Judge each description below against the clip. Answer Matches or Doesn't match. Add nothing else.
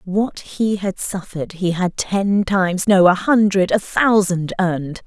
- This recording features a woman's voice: Matches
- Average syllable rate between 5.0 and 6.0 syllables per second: Doesn't match